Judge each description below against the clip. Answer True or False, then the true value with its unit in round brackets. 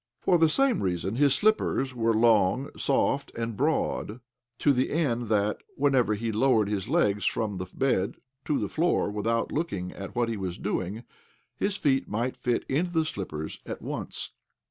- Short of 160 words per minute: False (170 wpm)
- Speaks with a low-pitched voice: True (115 Hz)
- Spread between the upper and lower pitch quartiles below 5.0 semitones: False (5.5 semitones)